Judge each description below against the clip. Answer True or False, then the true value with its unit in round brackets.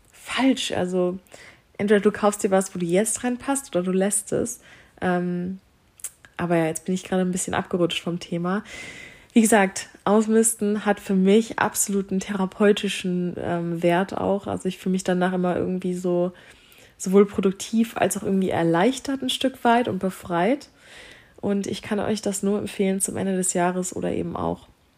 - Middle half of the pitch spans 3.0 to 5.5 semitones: False (2.6 semitones)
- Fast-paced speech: False (170 wpm)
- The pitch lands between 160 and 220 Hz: True (190 Hz)